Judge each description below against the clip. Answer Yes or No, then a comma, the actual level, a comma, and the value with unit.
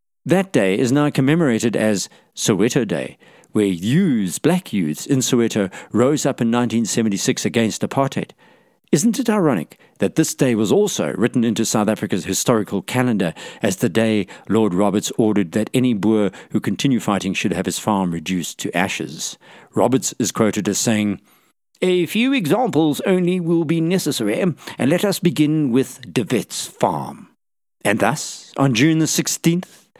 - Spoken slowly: No, average, 160 wpm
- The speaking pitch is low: Yes, low, 125 Hz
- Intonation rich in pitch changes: Yes, wide, 6.8 semitones